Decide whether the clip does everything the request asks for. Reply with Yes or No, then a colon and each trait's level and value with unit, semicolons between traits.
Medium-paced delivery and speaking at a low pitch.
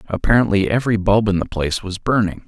Yes: average, 195 wpm; low, 100 Hz